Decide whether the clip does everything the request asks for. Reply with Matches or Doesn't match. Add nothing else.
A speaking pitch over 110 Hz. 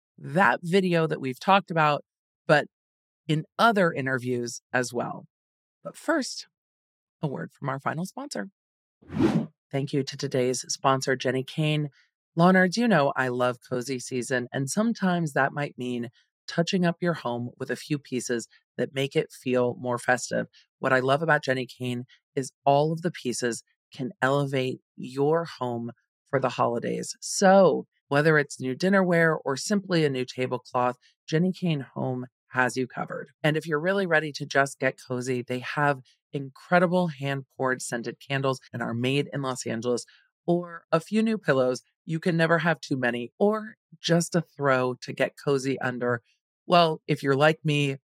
Matches